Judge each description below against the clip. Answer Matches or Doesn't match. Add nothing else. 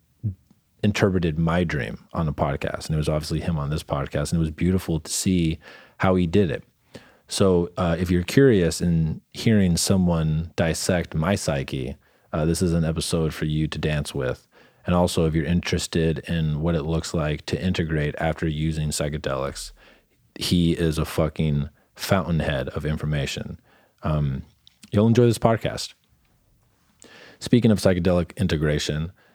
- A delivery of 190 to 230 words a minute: Doesn't match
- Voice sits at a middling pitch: Doesn't match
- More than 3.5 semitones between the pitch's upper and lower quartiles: Doesn't match